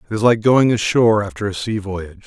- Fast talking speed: Yes, fast, 240 wpm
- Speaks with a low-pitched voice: Yes, low, 105 Hz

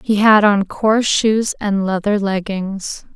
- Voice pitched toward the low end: No, high, 205 Hz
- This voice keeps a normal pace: Yes, average, 150 wpm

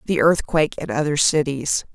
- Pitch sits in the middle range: Yes, medium, 145 Hz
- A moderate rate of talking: Yes, average, 155 wpm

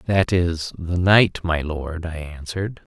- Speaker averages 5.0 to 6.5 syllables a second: No, 3.8 syllables/s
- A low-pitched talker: Yes, very low, 85 Hz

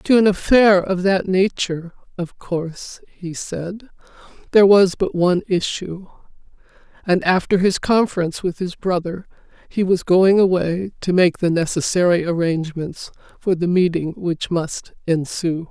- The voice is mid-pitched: Yes, medium, 180 Hz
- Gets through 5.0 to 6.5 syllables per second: No, 4.5 syllables/s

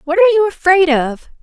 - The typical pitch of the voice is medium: No, very high, 345 Hz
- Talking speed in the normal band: No, fast, 210 wpm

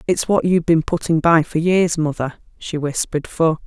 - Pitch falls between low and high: Yes, medium, 160 Hz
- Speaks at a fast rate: No, average, 195 wpm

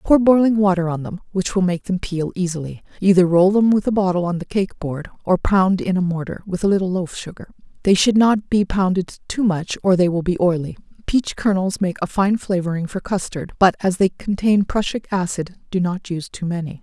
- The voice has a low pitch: No, medium, 185 Hz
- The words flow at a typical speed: No, fast, 220 wpm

